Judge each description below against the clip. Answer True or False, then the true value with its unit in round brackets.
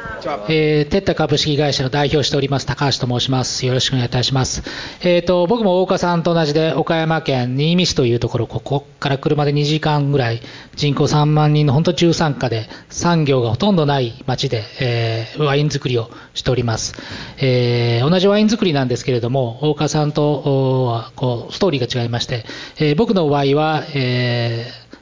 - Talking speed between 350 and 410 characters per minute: True (360 characters per minute)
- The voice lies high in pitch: False (140 Hz)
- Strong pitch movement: False (3.6 semitones)